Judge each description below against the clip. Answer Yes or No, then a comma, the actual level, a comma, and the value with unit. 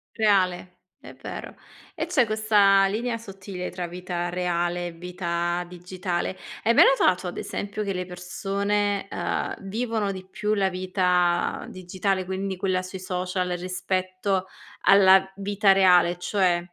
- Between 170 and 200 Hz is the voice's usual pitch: Yes, medium, 185 Hz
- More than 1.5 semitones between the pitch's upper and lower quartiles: Yes, narrow, 1.9 semitones